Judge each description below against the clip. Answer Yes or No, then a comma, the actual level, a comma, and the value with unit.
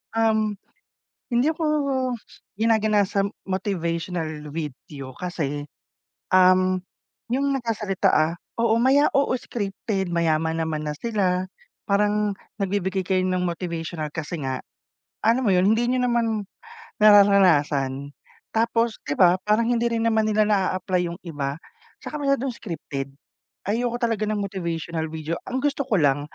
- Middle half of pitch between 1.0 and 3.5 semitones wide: No, average, 5.2 semitones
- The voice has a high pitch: Yes, high, 195 Hz